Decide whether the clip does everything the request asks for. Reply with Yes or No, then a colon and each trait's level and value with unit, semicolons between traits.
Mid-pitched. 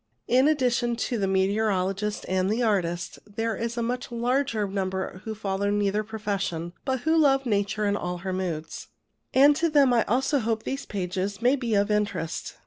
No: high, 210 Hz